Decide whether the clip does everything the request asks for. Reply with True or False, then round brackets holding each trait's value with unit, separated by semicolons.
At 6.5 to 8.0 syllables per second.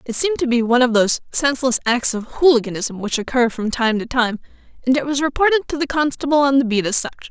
True (6.6 syllables/s)